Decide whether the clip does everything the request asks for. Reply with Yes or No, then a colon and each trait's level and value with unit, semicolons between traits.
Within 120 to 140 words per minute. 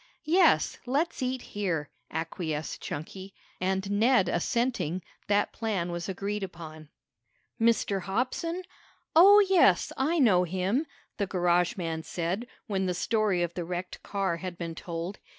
Yes: slow, 135 wpm